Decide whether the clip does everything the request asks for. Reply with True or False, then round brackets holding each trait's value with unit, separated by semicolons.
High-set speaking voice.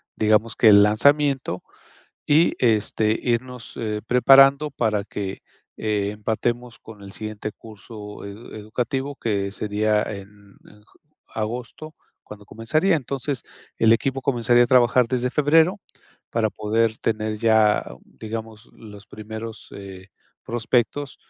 False (110 Hz)